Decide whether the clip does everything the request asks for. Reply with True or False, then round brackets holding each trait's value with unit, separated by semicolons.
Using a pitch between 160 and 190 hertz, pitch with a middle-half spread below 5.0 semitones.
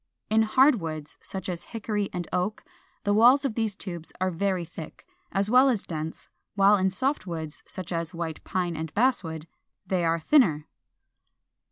True (185 Hz; 4.5 semitones)